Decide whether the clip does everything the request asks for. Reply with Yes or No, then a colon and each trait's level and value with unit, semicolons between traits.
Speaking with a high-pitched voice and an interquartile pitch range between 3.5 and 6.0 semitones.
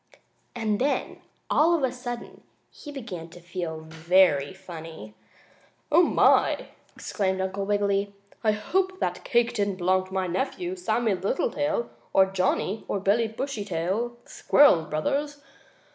Yes: high, 200 Hz; average, 4.8 semitones